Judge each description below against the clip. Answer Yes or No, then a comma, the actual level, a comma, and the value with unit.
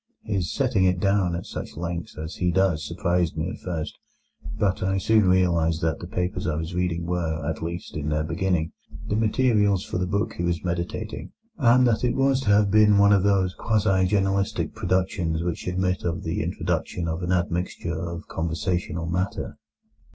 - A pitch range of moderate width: Yes, average, 3.0 semitones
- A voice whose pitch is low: Yes, very low, 90 Hz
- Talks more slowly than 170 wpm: No, average, 185 wpm